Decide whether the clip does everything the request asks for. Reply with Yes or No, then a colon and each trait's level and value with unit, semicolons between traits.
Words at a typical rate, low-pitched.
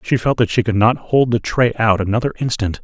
No: fast, 255 wpm; low, 115 Hz